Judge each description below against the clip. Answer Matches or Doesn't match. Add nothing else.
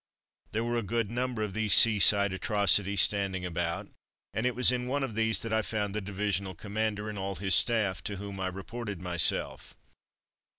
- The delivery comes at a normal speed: Matches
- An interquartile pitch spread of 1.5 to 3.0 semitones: Matches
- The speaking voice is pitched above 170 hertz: Doesn't match